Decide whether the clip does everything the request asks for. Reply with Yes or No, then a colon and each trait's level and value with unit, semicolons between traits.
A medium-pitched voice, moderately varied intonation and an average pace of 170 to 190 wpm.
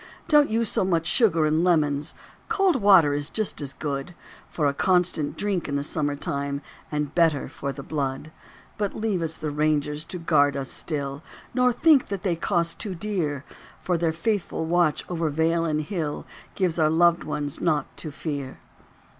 Yes: medium, 160 Hz; average, 3.8 semitones; average, 180 wpm